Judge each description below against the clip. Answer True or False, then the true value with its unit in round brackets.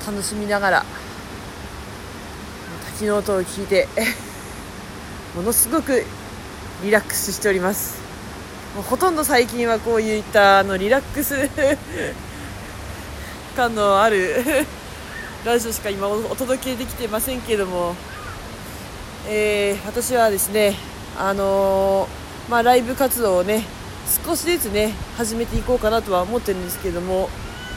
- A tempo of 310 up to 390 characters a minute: False (260 characters per minute)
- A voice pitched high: True (200 Hz)